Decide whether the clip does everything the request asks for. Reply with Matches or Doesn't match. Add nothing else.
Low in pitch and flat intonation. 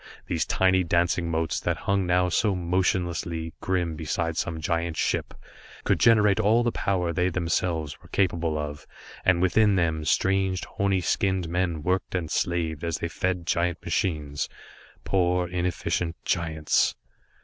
Matches